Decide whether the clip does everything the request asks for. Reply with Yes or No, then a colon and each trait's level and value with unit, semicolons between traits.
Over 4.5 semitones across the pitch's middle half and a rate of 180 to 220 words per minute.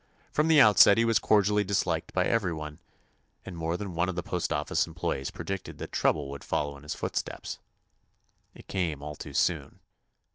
Yes: average, 5.1 semitones; average, 185 wpm